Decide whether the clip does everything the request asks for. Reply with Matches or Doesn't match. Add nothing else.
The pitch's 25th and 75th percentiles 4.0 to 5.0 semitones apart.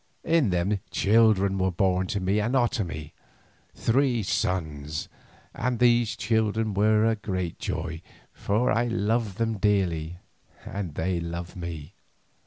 Matches